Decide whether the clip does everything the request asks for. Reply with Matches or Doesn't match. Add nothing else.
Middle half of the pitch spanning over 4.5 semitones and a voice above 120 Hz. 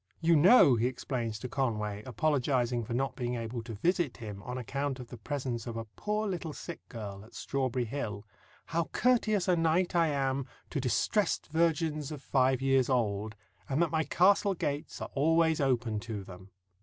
Matches